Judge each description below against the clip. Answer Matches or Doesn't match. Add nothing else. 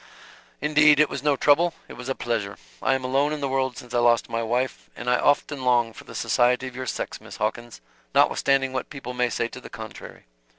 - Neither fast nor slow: Doesn't match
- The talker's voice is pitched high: Doesn't match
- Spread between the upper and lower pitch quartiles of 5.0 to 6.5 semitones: Doesn't match